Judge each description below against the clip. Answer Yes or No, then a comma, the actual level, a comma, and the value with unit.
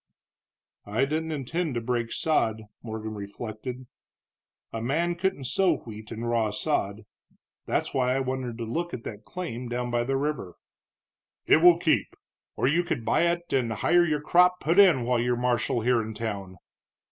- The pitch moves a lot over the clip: Yes, wide, 5.8 semitones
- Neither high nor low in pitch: No, low, 125 Hz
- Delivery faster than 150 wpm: Yes, average, 170 wpm